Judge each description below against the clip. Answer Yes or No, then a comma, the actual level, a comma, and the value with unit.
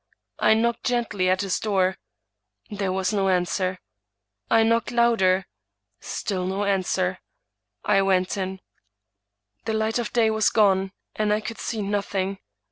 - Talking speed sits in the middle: Yes, average, 145 wpm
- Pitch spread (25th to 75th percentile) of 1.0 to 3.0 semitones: Yes, narrow, 2.6 semitones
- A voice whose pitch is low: No, high, 200 Hz